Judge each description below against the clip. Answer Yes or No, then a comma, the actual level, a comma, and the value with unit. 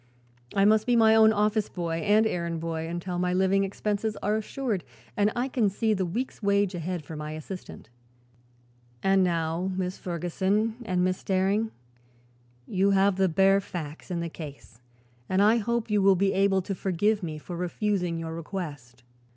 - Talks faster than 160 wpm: Yes, average, 175 wpm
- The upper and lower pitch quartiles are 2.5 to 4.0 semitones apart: Yes, average, 3.4 semitones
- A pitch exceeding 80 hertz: Yes, high, 190 Hz